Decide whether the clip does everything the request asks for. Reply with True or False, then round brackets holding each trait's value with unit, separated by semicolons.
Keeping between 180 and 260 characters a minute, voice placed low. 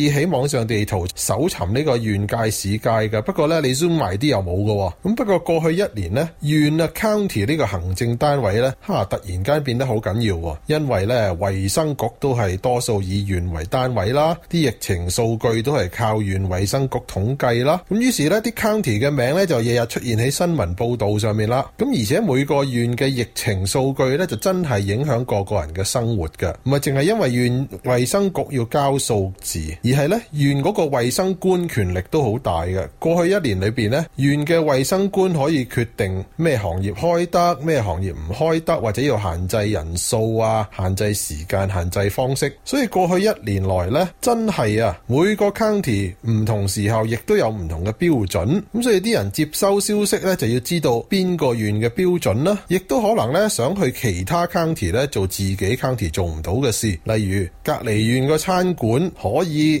False (310 characters per minute; 125 Hz)